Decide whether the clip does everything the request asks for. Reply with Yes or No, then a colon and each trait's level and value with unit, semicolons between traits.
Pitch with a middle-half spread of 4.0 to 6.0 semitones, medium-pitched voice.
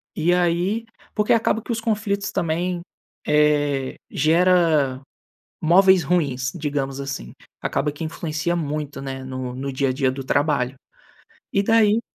Yes: average, 4.8 semitones; medium, 155 Hz